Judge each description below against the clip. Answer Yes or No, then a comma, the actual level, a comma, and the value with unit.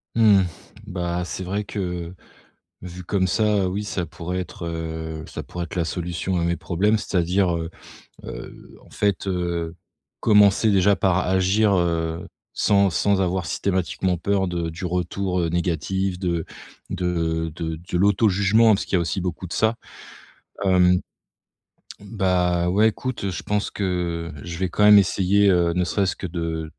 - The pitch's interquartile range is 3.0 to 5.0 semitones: No, narrow, 2.5 semitones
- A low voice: Yes, very low, 90 Hz